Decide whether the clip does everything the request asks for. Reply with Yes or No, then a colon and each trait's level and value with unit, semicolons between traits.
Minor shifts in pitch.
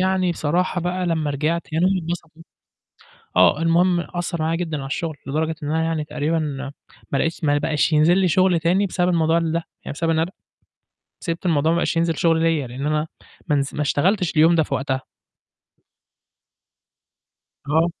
Yes: narrow, 2.2 semitones